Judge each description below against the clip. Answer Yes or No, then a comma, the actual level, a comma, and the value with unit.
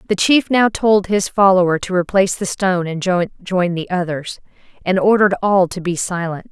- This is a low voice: No, medium, 185 Hz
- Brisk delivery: No, average, 185 wpm